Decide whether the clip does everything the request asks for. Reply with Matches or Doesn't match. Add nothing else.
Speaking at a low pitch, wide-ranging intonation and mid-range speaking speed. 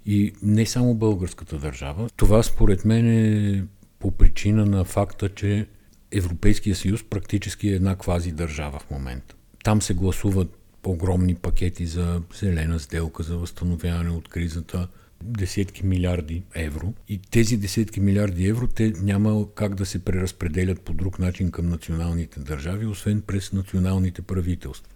Doesn't match